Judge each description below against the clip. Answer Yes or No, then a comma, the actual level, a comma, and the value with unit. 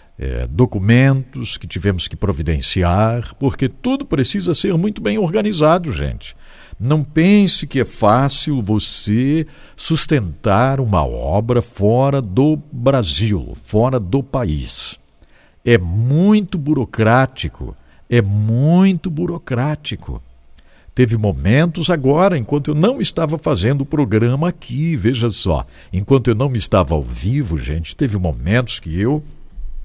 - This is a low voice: Yes, low, 125 Hz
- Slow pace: Yes, slow, 120 wpm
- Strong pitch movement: Yes, wide, 7.2 semitones